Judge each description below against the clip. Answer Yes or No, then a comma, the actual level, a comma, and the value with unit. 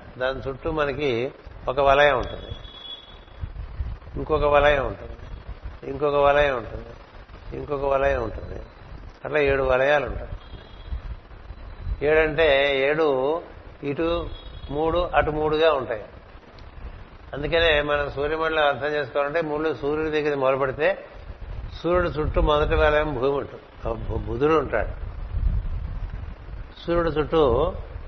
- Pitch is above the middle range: No, low, 135 Hz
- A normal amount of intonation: No, wide, 7.7 semitones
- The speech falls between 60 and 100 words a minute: Yes, average, 95 wpm